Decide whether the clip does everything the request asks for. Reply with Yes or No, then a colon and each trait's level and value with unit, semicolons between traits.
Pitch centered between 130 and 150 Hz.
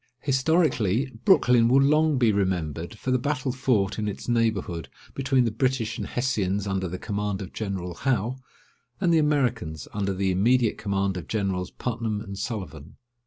No: low, 110 Hz